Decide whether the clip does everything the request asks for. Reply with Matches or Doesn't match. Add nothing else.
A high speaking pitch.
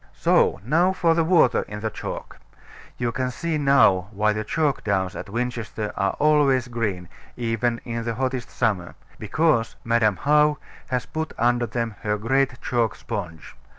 Doesn't match